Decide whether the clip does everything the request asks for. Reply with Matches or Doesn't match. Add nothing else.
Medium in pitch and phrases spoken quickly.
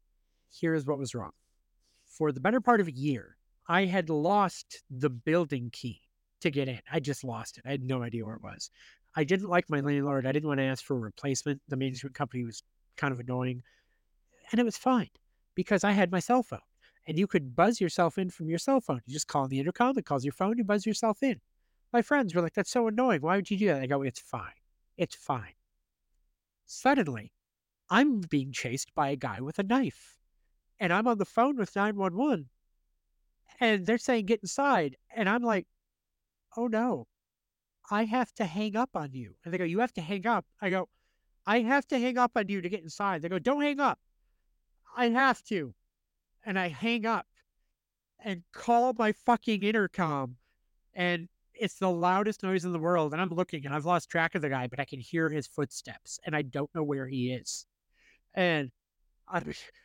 Matches